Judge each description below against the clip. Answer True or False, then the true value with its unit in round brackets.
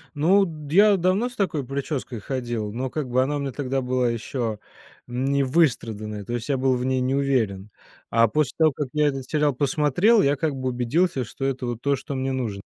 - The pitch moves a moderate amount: True (3.3 semitones)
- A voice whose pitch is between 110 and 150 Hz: True (135 Hz)